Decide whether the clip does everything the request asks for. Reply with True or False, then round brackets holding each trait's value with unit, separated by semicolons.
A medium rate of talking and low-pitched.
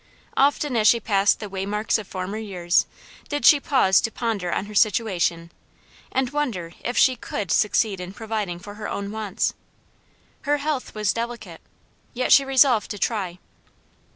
False (160 wpm; 215 Hz)